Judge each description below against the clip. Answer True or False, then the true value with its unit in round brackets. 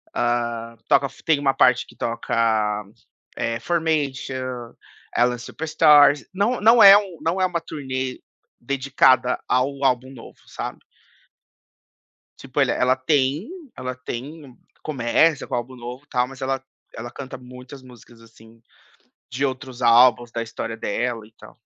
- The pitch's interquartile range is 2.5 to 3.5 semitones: True (3.0 semitones)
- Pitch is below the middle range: True (130 Hz)